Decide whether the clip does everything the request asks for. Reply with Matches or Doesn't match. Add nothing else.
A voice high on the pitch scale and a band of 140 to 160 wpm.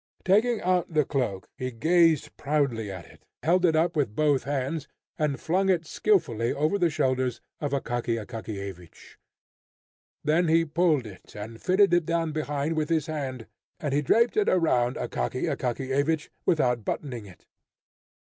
Doesn't match